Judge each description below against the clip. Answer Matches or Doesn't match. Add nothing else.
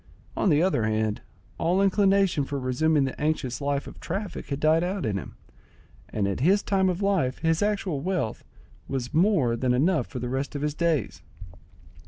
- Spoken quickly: Doesn't match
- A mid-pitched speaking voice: Matches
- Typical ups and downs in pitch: Doesn't match